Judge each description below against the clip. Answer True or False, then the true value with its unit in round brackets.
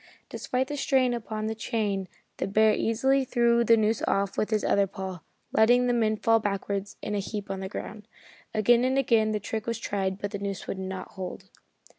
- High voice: True (215 Hz)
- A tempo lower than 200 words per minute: False (205 wpm)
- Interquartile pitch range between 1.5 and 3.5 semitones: True (2.9 semitones)